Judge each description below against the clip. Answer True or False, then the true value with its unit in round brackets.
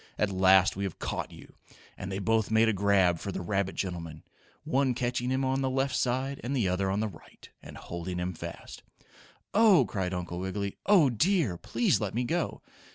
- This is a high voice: False (105 Hz)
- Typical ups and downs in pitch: False (5.7 semitones)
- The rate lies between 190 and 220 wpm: True (200 wpm)